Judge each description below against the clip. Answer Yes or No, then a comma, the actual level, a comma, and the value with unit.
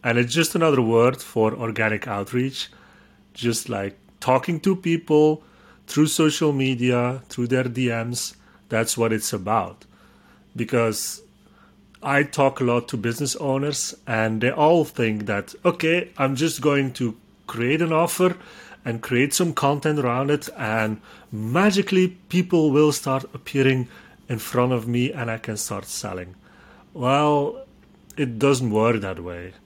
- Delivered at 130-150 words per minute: Yes, average, 145 wpm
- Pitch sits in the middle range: No, low, 130 Hz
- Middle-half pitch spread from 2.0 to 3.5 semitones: No, average, 4.8 semitones